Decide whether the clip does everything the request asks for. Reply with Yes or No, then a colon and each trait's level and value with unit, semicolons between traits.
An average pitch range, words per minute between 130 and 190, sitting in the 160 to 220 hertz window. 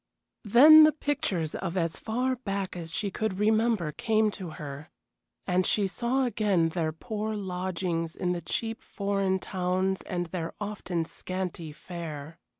Yes: average, 4.2 semitones; average, 150 wpm; high, 190 Hz